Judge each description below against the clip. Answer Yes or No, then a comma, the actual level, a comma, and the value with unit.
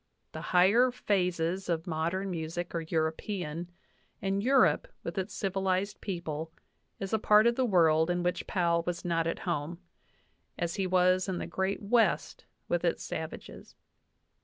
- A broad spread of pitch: No, average, 2.7 semitones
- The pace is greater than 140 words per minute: Yes, average, 160 wpm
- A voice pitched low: No, medium, 180 Hz